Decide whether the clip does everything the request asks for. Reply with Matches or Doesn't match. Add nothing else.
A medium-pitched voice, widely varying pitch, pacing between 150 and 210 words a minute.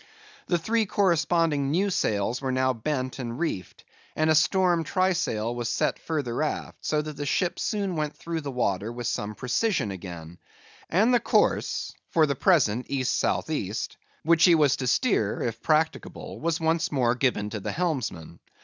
Matches